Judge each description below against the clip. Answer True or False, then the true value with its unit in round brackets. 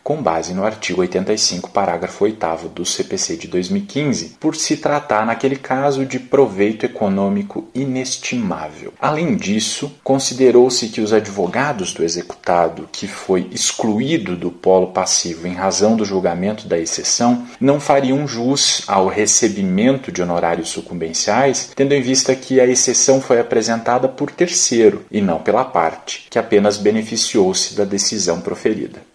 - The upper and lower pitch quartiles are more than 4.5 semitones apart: True (5.3 semitones)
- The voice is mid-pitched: False (115 Hz)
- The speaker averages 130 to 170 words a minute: True (140 wpm)